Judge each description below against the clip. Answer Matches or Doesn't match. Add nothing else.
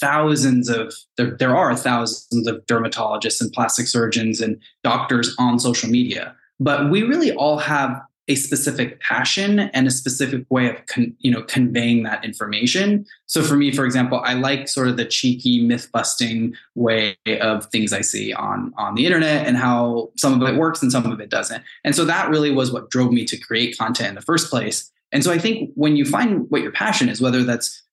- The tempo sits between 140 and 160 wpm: Doesn't match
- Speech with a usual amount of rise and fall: Matches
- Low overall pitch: Matches